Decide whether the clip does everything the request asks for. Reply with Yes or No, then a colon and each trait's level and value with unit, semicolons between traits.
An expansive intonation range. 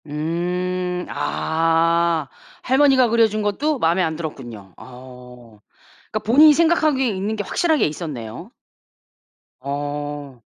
Yes: wide, 7.3 semitones